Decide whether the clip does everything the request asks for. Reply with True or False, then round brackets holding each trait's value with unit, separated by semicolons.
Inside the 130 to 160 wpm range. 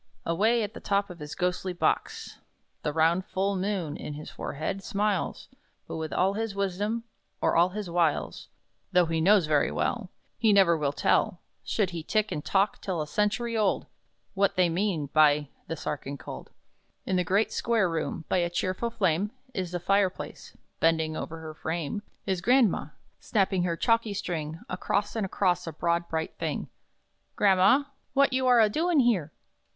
False (175 wpm)